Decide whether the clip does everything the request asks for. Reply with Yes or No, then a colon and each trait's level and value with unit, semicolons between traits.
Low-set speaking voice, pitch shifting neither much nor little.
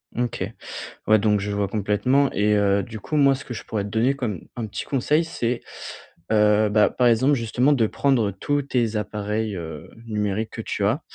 Yes: low, 110 Hz; average, 3.4 semitones